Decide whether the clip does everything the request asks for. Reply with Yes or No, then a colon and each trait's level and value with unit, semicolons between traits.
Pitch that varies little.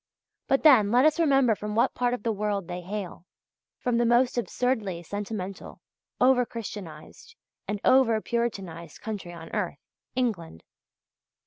No: average, 4.5 semitones